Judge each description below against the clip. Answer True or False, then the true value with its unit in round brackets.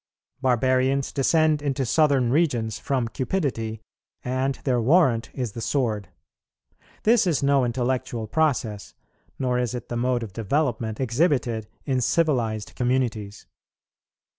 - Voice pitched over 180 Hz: False (125 Hz)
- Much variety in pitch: False (3.4 semitones)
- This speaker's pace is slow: True (120 wpm)